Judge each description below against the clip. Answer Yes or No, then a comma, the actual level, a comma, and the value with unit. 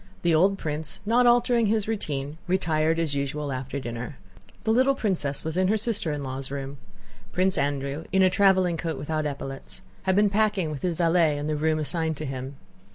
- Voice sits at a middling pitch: Yes, medium, 160 Hz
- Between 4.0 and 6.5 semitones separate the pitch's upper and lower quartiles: Yes, average, 5.1 semitones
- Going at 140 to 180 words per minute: No, average, 195 wpm